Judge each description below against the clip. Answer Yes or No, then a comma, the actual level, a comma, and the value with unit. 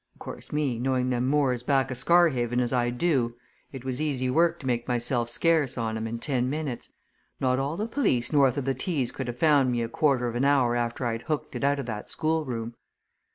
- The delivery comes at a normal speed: No, fast, 225 wpm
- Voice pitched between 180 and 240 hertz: No, low, 130 Hz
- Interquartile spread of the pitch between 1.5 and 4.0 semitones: Yes, average, 3.1 semitones